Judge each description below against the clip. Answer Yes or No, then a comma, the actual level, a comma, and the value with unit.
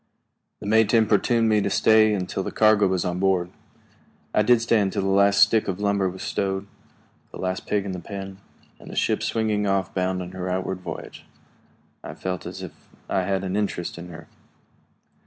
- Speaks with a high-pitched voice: No, very low, 95 Hz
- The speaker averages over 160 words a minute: Yes, average, 195 wpm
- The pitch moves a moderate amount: No, narrow, 2.1 semitones